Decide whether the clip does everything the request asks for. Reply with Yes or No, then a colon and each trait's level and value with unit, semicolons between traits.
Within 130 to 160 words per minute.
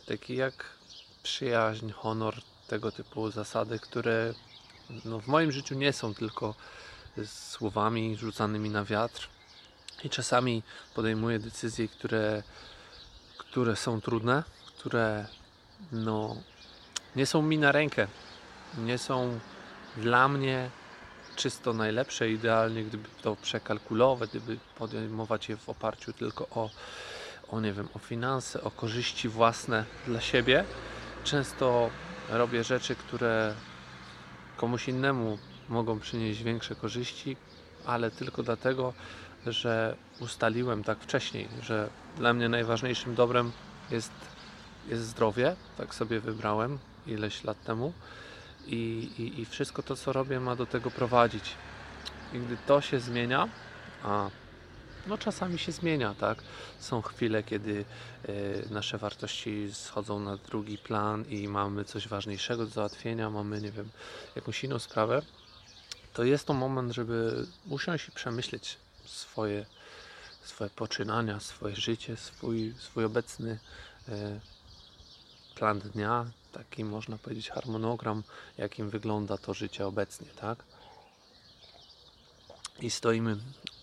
No: average, 120 wpm